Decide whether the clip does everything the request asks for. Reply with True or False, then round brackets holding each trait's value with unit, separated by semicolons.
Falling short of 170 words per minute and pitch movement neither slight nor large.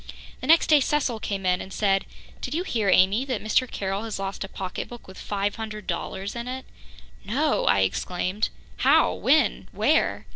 False (180 wpm; 4.5 semitones)